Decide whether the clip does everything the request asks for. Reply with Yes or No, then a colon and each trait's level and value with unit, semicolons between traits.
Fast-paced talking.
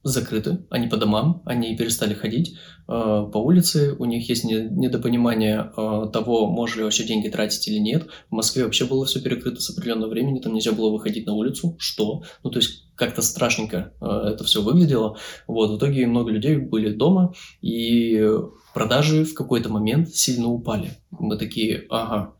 Yes: fast, 175 wpm